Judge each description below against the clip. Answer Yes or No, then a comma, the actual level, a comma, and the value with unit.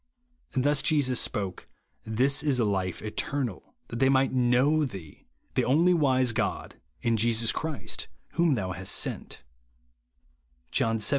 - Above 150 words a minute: No, average, 140 wpm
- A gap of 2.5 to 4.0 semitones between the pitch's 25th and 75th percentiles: No, average, 4.5 semitones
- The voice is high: No, low, 125 Hz